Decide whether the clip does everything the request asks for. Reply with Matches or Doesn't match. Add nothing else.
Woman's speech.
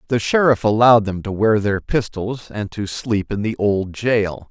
Doesn't match